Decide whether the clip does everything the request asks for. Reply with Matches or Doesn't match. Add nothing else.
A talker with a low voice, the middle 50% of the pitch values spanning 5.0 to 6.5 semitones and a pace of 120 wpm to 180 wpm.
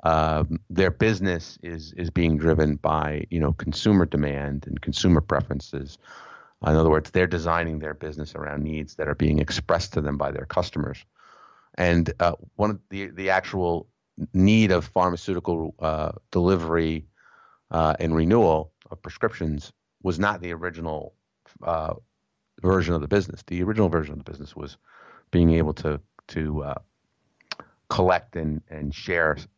Doesn't match